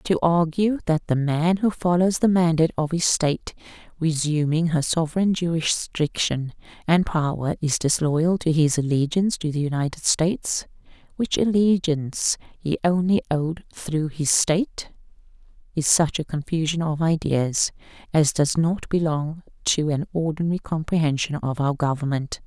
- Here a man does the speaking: No, female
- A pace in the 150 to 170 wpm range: No, average, 140 wpm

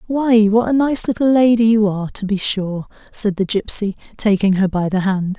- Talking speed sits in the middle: No, fast, 210 wpm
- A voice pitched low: No, high, 210 Hz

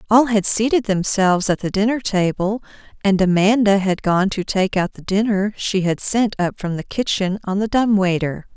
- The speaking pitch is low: No, high, 200 Hz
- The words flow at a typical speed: Yes, average, 195 wpm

